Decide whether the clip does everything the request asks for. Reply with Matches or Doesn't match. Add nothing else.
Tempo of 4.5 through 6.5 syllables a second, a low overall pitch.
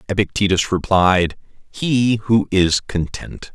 Doesn't match